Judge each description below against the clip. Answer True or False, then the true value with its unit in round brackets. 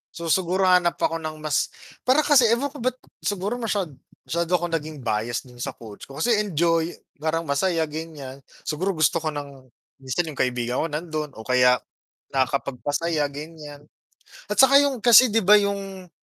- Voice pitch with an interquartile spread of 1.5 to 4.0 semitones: False (5.5 semitones)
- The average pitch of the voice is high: False (165 Hz)